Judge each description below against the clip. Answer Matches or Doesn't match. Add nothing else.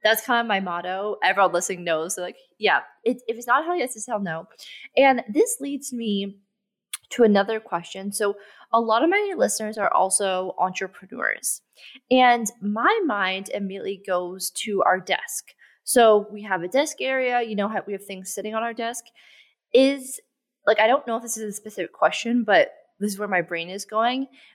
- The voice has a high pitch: Matches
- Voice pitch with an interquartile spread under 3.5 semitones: Doesn't match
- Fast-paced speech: Doesn't match